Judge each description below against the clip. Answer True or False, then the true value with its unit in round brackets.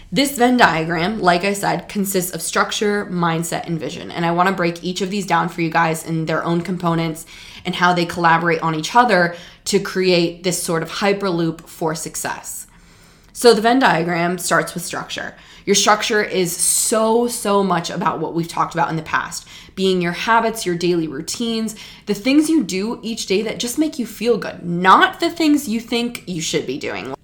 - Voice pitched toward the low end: False (180 Hz)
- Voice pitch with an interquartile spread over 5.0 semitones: False (4.5 semitones)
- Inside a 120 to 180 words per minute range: False (200 wpm)